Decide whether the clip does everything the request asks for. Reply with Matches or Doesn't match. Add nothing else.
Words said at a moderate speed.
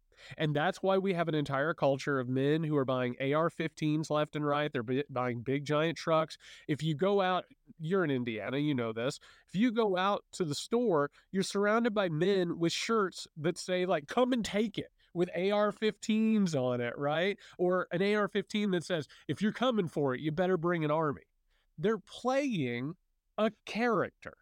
Matches